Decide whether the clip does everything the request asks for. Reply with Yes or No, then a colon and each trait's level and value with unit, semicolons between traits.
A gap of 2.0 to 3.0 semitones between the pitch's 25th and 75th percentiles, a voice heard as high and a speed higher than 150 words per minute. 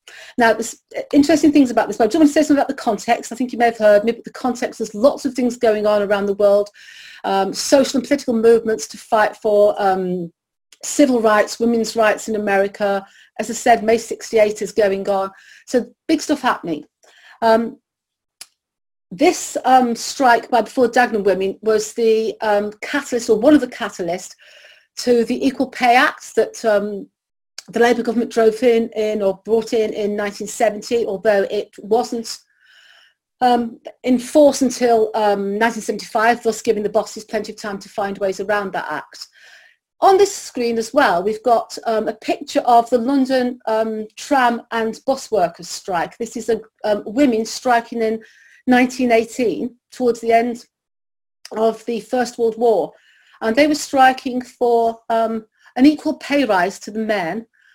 Yes: average, 2.7 semitones; high, 230 Hz; average, 170 wpm